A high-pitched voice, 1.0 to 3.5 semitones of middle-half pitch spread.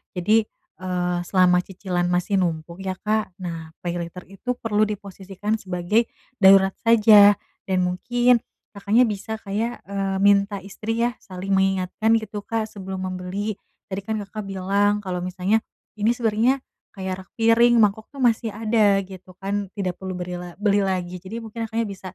Yes: high, 195 Hz; average, 2.9 semitones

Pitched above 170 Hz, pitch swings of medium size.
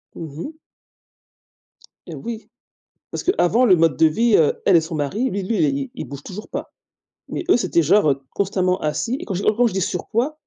No: medium, 185 Hz; wide, 6.2 semitones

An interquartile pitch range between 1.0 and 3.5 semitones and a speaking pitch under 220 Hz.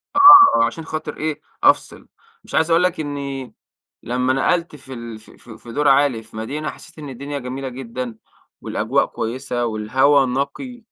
No: average, 4.1 semitones; low, 135 Hz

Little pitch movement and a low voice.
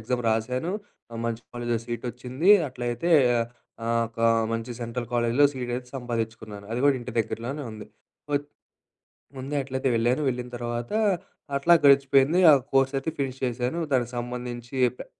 Yes: narrow, 2.3 semitones; low, 125 Hz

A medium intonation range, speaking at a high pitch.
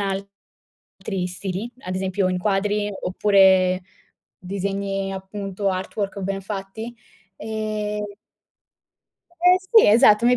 No: narrow, 1.6 semitones; high, 195 Hz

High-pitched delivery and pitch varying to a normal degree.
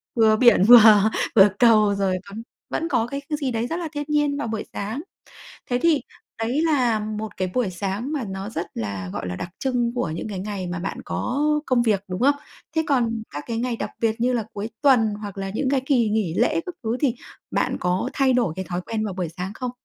Yes: high, 225 Hz; average, 4.5 semitones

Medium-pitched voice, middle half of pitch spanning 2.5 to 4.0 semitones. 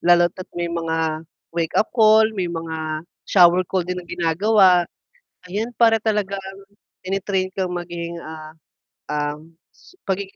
Yes: medium, 175 Hz; average, 3.0 semitones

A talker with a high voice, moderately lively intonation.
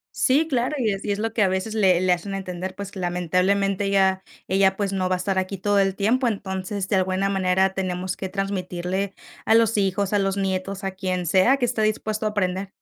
No: high, 195 Hz; narrow, 1.6 semitones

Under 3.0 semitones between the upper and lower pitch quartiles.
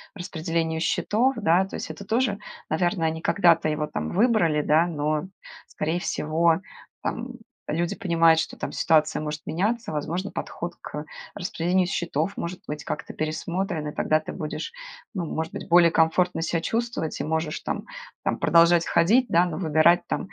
Yes: narrow, 2.6 semitones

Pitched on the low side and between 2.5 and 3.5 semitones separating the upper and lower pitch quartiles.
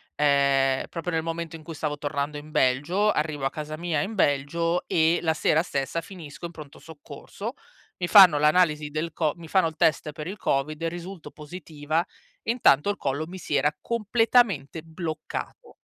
No: medium, 160 Hz; average, 2.8 semitones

